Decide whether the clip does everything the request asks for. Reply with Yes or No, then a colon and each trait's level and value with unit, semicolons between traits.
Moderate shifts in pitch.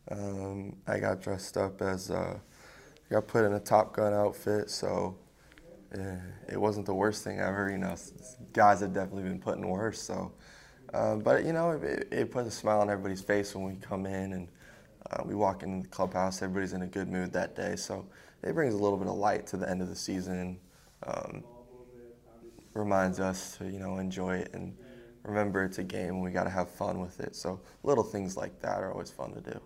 No: narrow, 2.1 semitones